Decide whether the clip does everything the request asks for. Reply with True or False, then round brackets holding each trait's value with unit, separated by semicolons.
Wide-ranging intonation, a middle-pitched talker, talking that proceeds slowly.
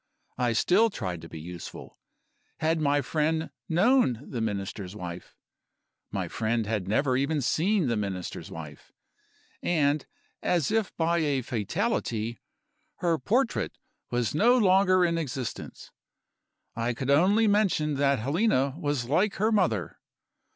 True (7.8 semitones; 145 Hz; 130 wpm)